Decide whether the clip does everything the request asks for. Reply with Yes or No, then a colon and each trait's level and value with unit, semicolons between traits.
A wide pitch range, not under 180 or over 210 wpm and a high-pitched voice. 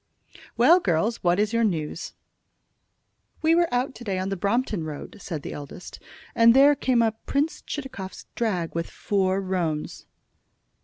No: wide, 5.7 semitones; average, 155 wpm; high, 205 Hz